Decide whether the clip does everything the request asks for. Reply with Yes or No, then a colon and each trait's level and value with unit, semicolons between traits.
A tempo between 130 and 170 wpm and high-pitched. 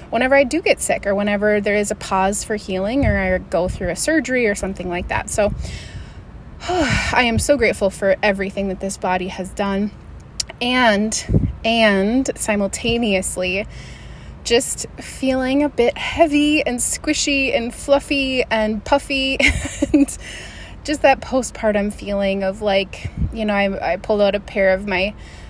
Yes: average, 160 wpm; high, 215 Hz